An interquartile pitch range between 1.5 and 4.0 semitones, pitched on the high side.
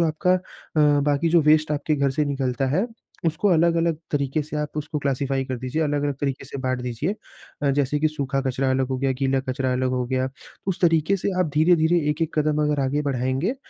No: average, 2.8 semitones; medium, 145 Hz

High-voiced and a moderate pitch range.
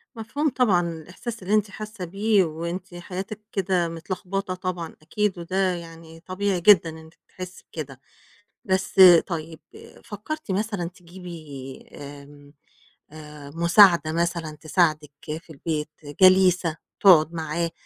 No: medium, 175 Hz; average, 3.1 semitones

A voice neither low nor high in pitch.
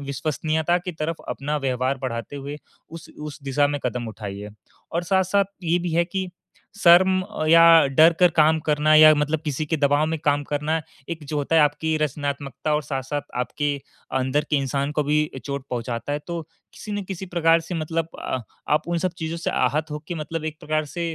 Yes: medium, 150 Hz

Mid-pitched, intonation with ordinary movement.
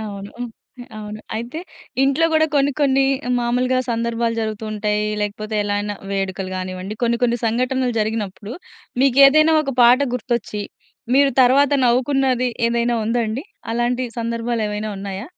No: high, 235 Hz; average, 3.3 semitones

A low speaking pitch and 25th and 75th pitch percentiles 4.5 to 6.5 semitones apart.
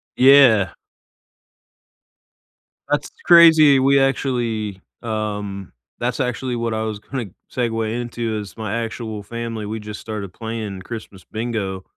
No: low, 115 Hz; narrow, 2.5 semitones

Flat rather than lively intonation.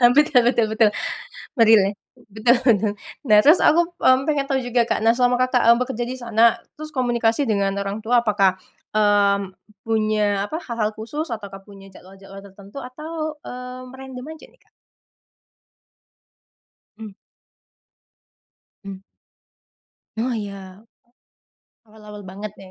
No: average, 3.8 semitones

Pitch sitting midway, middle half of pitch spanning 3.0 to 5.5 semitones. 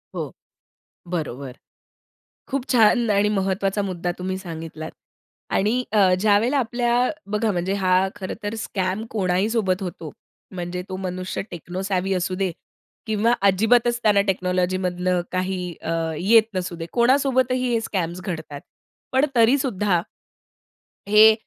No: high, 195 Hz; average, 3.5 semitones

